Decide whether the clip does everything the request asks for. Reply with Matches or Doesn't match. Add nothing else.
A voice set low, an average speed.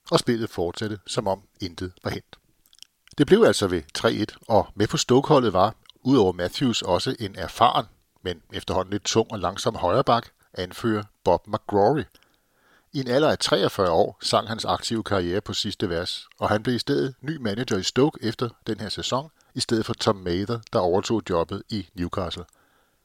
Matches